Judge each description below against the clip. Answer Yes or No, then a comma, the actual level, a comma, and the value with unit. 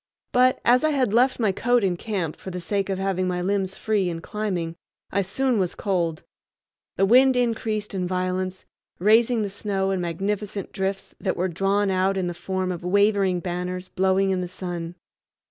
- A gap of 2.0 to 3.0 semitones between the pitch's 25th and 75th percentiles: Yes, narrow, 2.4 semitones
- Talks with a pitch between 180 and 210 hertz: Yes, high, 190 Hz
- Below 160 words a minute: No, average, 185 wpm